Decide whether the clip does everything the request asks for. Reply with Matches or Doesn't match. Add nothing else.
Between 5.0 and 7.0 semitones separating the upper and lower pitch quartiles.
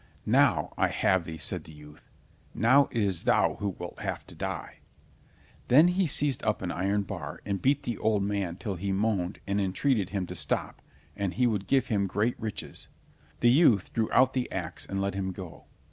Doesn't match